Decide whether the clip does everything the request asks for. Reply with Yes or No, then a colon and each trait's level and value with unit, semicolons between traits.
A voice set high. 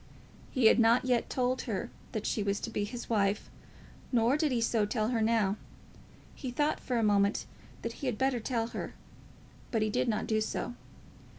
Yes: high, 230 Hz